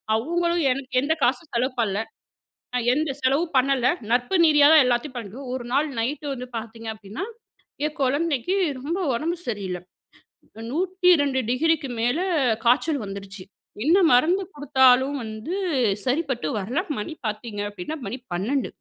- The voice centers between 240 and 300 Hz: Yes, very high, 260 Hz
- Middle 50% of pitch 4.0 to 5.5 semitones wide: Yes, average, 4.8 semitones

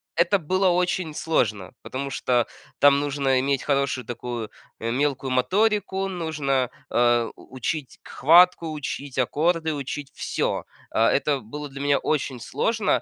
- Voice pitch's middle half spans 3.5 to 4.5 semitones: Yes, average, 4.2 semitones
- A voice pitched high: No, medium, 140 Hz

